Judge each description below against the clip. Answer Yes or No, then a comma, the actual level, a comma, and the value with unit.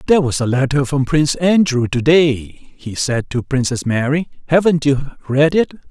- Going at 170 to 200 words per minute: Yes, average, 175 wpm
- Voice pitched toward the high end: No, medium, 145 Hz